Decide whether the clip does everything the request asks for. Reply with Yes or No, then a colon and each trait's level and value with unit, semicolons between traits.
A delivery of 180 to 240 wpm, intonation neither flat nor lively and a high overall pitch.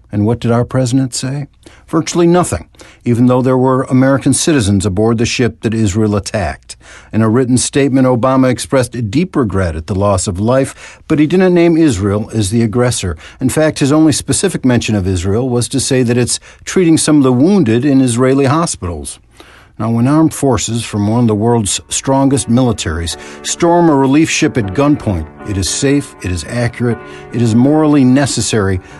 No: average, 185 wpm; average, 4.5 semitones; low, 120 Hz